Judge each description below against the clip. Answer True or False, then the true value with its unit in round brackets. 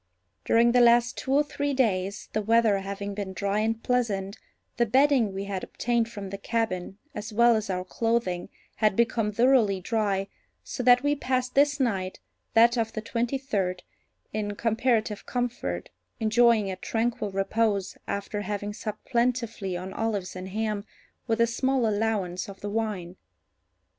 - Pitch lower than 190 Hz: False (220 Hz)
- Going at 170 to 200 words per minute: False (160 wpm)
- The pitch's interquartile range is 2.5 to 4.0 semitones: True (3.1 semitones)